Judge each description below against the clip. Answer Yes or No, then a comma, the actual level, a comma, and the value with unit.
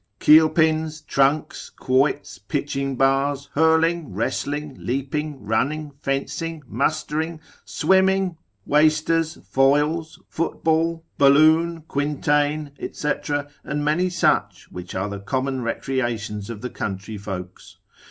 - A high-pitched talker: No, medium, 145 Hz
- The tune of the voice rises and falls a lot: No, average, 3.3 semitones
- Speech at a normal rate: No, slow, 100 wpm